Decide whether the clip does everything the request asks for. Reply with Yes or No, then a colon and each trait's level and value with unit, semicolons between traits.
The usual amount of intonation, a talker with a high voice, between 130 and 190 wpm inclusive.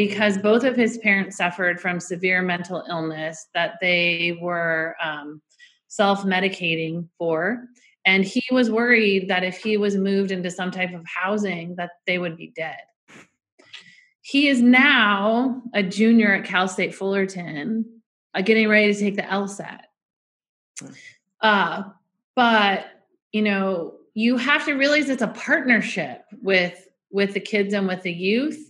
Yes: average, 3.8 semitones; high, 195 Hz; average, 145 wpm